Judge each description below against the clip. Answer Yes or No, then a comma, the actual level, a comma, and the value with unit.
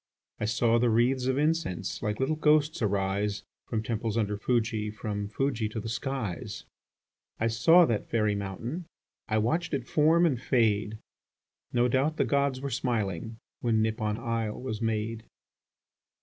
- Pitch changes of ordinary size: Yes, average, 3.7 semitones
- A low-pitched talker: Yes, low, 115 Hz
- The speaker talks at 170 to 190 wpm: No, average, 150 wpm